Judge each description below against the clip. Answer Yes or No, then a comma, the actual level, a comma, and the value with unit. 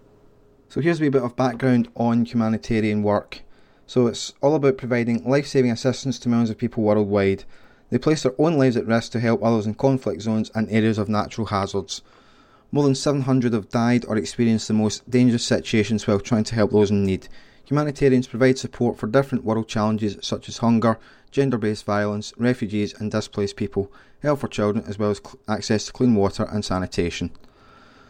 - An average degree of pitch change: Yes, average, 3.5 semitones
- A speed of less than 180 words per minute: No, average, 185 wpm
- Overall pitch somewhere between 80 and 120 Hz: Yes, low, 115 Hz